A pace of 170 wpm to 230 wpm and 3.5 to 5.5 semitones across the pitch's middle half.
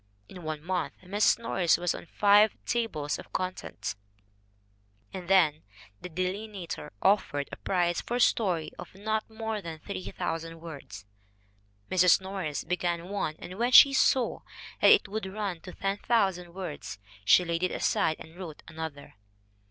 No: average, 150 wpm; average, 3.9 semitones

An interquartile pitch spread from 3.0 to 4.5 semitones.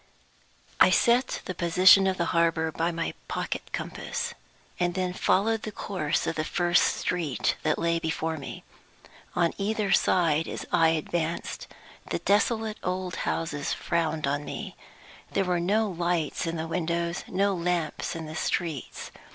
No: narrow, 2.4 semitones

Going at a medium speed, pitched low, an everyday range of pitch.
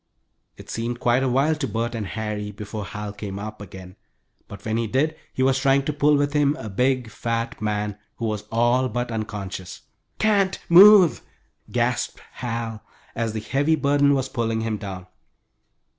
Yes: average, 175 wpm; low, 115 Hz; average, 4.4 semitones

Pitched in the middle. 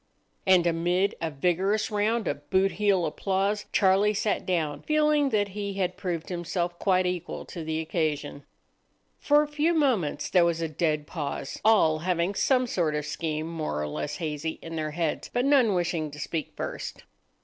Yes: medium, 175 Hz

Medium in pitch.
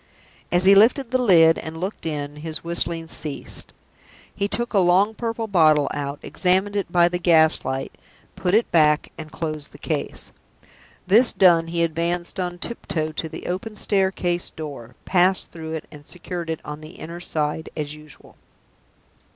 Yes: medium, 170 Hz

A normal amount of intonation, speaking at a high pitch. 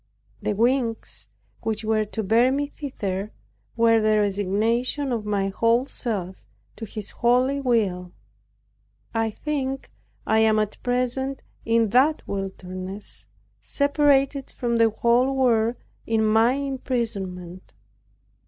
Yes: average, 3.6 semitones; high, 230 Hz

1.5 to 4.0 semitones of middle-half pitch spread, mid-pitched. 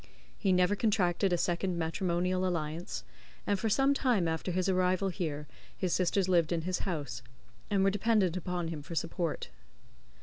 Yes: narrow, 2.5 semitones; medium, 180 Hz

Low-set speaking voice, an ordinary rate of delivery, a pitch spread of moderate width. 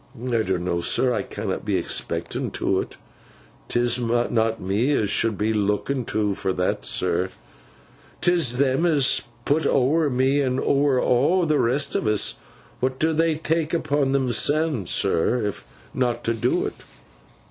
Yes: low, 125 Hz; average, 155 wpm; average, 4.6 semitones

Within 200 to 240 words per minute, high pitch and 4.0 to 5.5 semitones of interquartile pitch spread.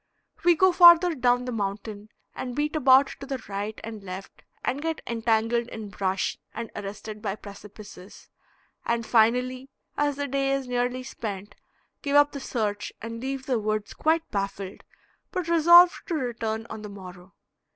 No: average, 160 wpm; high, 235 Hz; average, 4.8 semitones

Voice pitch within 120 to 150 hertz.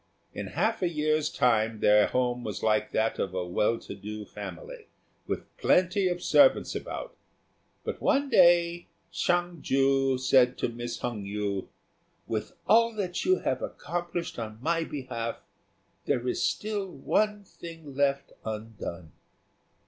Yes: low, 135 Hz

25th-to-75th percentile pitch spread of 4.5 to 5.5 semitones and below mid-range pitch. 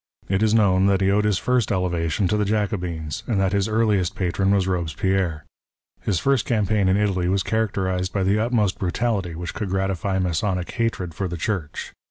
No: narrow, 2.5 semitones; very low, 95 Hz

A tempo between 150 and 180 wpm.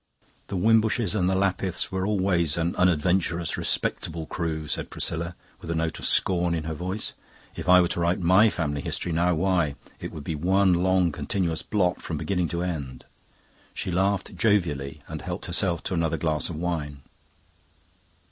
Yes: average, 175 wpm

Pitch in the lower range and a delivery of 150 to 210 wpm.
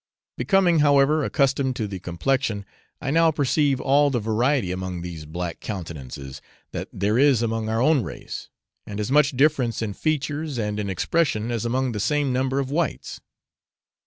Yes: low, 125 Hz; average, 165 wpm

